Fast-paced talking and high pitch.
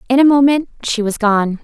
Yes: fast, 220 wpm; high, 245 Hz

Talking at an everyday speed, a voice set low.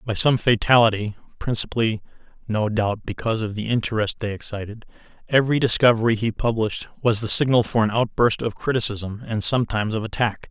Yes: average, 160 wpm; low, 110 Hz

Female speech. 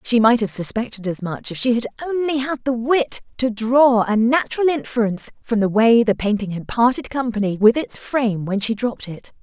Yes: female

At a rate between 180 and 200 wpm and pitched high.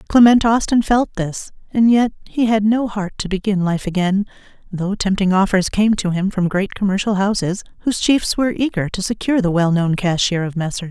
Yes: average, 195 wpm; high, 200 Hz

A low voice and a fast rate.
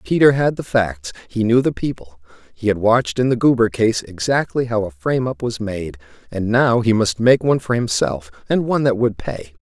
Yes: low, 115 Hz; fast, 220 wpm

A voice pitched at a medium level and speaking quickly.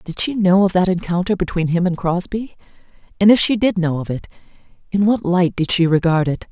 Yes: medium, 180 Hz; fast, 220 wpm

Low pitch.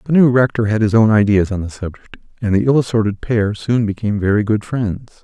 Yes: low, 110 Hz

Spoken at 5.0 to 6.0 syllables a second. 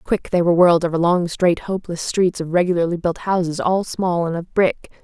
Yes: 5.6 syllables/s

